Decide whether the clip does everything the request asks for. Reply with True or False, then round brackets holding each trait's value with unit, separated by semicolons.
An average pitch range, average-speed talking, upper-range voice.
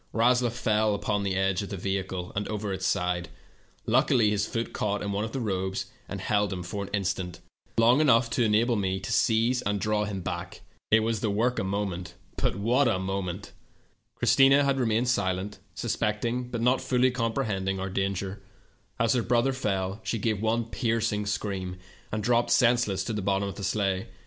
False (3.2 semitones; 155 wpm; 105 Hz)